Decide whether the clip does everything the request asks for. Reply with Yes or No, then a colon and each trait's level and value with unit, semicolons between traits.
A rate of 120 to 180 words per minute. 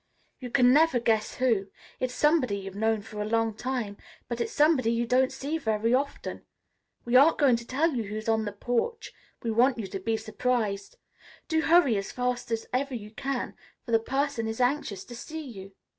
No: average, 200 wpm